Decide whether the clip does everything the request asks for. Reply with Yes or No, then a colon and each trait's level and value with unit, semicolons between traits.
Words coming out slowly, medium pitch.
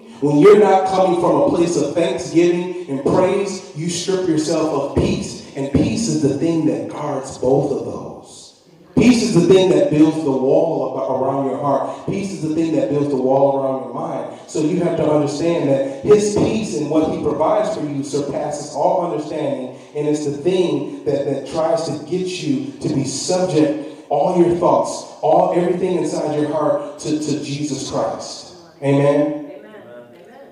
No: average, 180 wpm; medium, 155 Hz